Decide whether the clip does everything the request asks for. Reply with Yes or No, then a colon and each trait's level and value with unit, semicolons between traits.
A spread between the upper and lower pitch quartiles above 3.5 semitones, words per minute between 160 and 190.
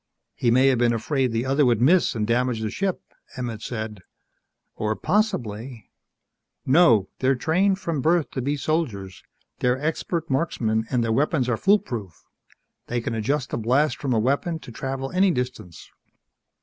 Yes: average, 5.1 semitones; average, 165 wpm